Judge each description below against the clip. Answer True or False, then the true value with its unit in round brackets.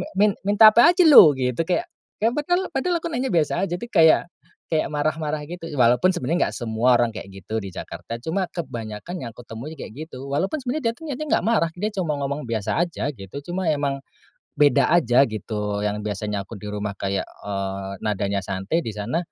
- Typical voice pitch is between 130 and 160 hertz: True (140 Hz)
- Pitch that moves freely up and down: True (8.6 semitones)